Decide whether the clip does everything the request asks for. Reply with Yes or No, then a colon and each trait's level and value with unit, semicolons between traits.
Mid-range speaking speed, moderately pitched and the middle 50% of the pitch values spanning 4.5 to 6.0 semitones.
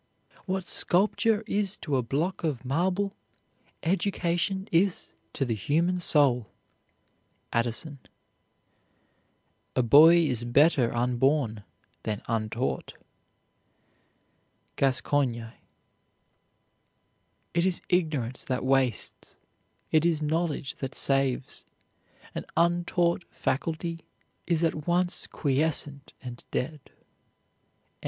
No: slow, 90 wpm; medium, 150 Hz; average, 5.2 semitones